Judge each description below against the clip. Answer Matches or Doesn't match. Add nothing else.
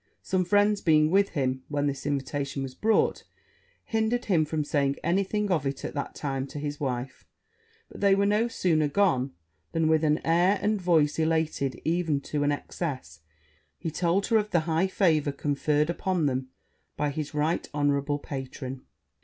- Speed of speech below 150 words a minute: Doesn't match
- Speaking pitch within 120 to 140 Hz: Doesn't match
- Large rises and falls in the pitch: Doesn't match